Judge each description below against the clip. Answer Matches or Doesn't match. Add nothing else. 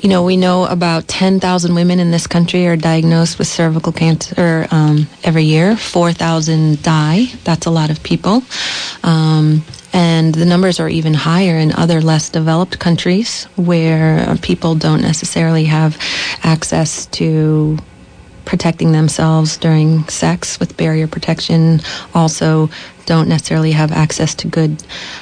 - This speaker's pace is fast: Doesn't match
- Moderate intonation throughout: Doesn't match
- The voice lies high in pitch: Doesn't match